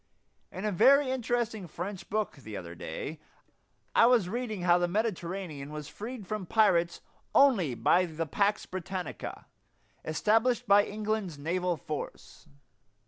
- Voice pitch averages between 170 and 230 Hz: Yes, high, 190 Hz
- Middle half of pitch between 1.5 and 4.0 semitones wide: No, average, 4.4 semitones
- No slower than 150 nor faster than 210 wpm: No, slow, 135 wpm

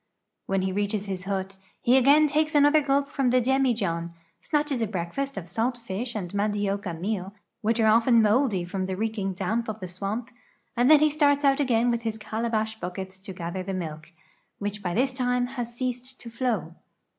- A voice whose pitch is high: Yes, high, 220 Hz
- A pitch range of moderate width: Yes, average, 4.9 semitones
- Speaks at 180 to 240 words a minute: Yes, average, 195 wpm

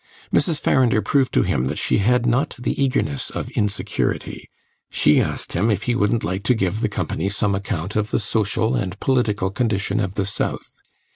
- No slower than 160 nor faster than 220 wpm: Yes, average, 190 wpm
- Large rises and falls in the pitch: No, average, 3.6 semitones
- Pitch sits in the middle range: No, low, 105 Hz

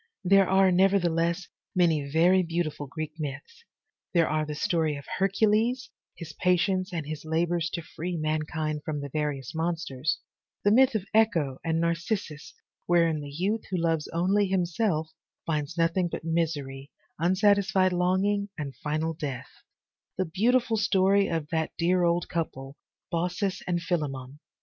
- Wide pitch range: No, average, 3.4 semitones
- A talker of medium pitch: Yes, medium, 170 Hz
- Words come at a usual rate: Yes, average, 145 wpm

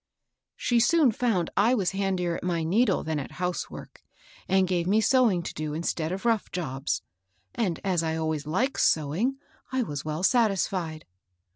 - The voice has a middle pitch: Yes, medium, 180 Hz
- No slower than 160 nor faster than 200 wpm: Yes, average, 180 wpm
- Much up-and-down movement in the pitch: Yes, wide, 5.7 semitones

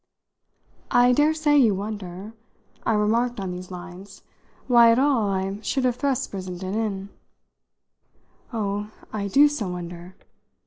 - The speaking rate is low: Yes, slow, 130 wpm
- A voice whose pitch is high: Yes, high, 210 Hz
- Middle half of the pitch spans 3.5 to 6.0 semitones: Yes, average, 4.4 semitones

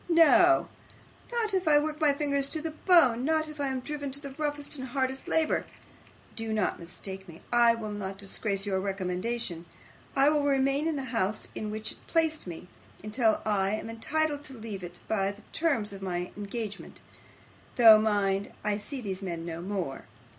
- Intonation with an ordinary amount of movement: No, wide, 6.7 semitones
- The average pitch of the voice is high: Yes, high, 230 Hz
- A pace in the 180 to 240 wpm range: Yes, average, 185 wpm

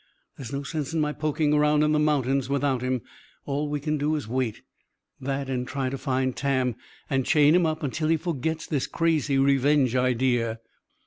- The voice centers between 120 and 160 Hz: Yes, medium, 140 Hz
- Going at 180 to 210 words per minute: Yes, average, 190 wpm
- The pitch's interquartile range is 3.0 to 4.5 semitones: No, narrow, 2.6 semitones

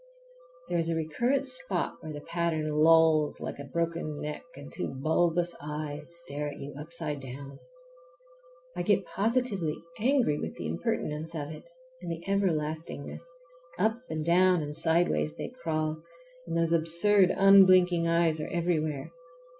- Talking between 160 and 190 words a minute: No, average, 145 wpm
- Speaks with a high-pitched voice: No, medium, 165 Hz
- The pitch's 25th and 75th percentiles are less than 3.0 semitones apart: Yes, narrow, 2.5 semitones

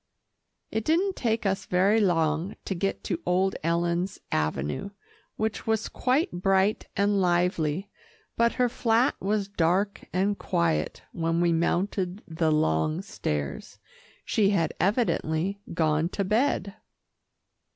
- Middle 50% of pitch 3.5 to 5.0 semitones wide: Yes, average, 3.9 semitones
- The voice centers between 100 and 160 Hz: No, medium, 185 Hz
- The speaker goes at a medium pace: No, slow, 125 wpm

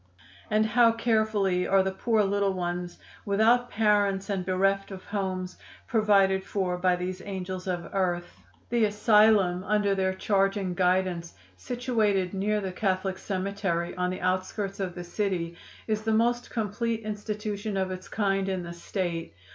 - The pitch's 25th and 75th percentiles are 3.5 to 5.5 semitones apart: No, narrow, 2.4 semitones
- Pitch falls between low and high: No, high, 195 Hz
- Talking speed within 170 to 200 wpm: No, average, 155 wpm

